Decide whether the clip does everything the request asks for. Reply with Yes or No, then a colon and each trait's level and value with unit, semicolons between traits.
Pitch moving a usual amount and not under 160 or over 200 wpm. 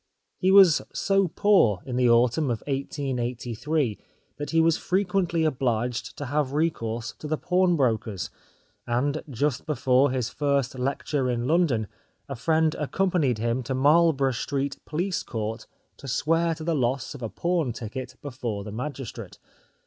No: average, 4.7 semitones; average, 150 wpm